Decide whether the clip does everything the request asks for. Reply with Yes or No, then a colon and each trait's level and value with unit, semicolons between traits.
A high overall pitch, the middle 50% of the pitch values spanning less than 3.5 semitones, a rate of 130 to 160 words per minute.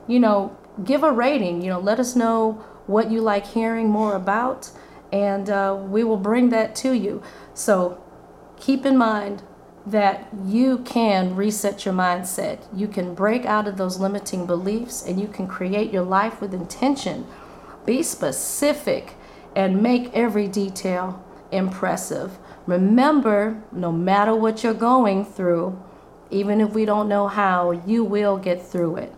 Yes: high, 205 Hz; average, 2.8 semitones; average, 155 wpm